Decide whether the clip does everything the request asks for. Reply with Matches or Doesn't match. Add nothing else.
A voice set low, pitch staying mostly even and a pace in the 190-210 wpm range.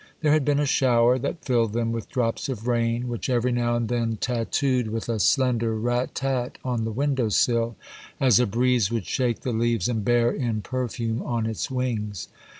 Matches